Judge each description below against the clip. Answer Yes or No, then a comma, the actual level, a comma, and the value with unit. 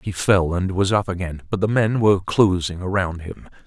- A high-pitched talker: No, very low, 95 Hz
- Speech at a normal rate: No, fast, 215 wpm